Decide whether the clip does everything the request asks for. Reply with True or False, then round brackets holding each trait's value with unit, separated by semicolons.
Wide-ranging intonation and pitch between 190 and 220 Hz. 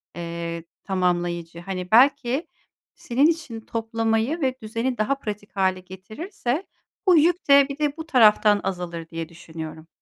True (7.6 semitones; 215 Hz)